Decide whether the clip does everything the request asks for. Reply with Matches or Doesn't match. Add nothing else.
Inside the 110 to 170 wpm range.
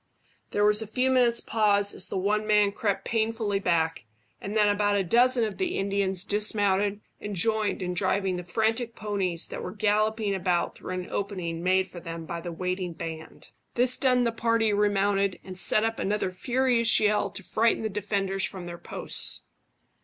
Doesn't match